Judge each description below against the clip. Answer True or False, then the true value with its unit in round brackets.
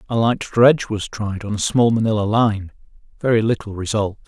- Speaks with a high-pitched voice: False (110 Hz)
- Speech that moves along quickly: False (170 wpm)